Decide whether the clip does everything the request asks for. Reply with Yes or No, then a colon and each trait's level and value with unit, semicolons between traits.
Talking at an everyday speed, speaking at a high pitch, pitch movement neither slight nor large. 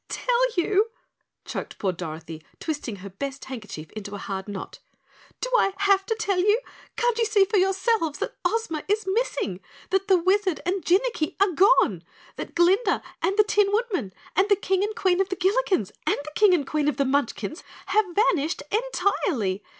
No: average, 180 wpm; very high, 370 Hz; wide, 6.9 semitones